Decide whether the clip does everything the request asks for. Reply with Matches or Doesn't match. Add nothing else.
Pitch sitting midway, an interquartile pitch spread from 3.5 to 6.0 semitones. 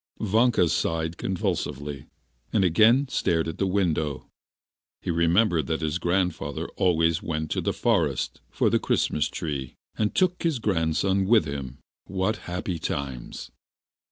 Doesn't match